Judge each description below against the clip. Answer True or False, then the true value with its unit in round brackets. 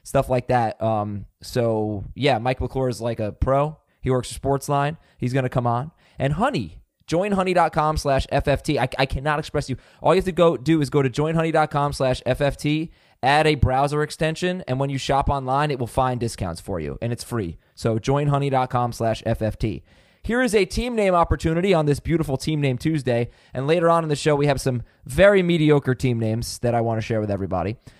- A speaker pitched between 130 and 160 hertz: True (135 Hz)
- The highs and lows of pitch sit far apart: False (4.3 semitones)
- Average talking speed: False (210 wpm)